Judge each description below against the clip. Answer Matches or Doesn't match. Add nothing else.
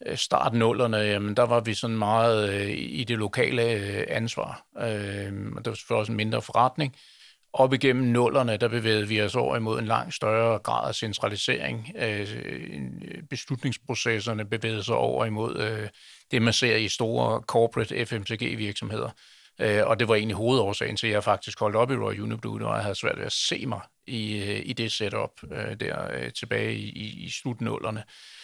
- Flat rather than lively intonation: Matches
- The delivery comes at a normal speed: Matches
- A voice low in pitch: Matches